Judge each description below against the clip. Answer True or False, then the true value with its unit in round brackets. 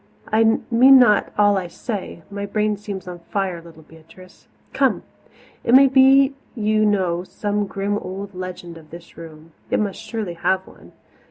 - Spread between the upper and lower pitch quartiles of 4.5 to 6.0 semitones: False (3.5 semitones)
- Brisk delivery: False (165 wpm)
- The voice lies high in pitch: True (200 Hz)